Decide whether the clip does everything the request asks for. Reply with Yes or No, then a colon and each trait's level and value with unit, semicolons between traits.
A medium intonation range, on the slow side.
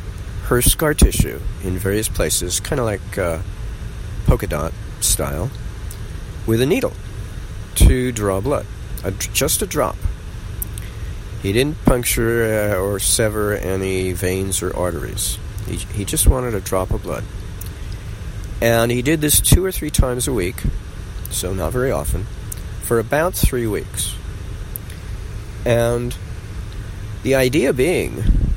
Yes: average, 3.1 semitones; slow, 130 wpm